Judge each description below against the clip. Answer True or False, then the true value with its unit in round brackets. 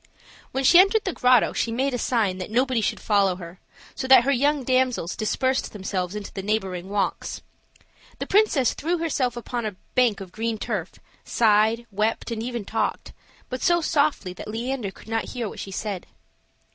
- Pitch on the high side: True (230 Hz)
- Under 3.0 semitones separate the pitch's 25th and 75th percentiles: False (4.2 semitones)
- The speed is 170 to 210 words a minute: True (185 wpm)